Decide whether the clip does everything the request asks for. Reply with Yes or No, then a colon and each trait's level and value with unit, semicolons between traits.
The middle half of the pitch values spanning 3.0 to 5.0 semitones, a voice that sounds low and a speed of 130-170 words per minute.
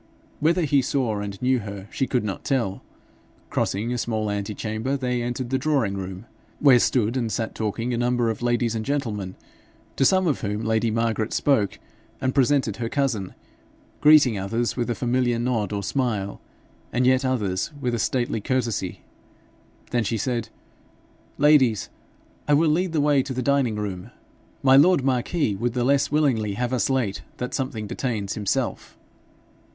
Yes: average, 3.7 semitones; low, 120 Hz; average, 165 wpm